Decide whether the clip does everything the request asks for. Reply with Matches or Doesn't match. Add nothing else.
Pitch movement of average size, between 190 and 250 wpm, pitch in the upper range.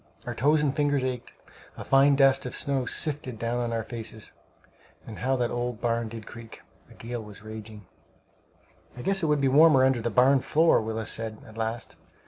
Doesn't match